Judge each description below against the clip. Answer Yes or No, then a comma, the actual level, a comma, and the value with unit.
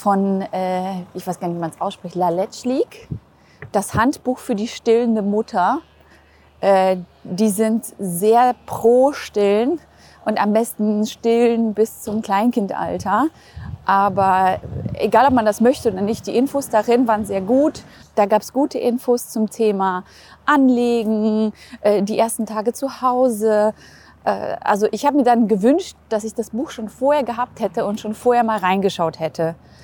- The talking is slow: No, average, 150 wpm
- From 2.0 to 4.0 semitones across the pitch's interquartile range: Yes, average, 3.5 semitones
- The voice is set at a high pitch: Yes, high, 220 Hz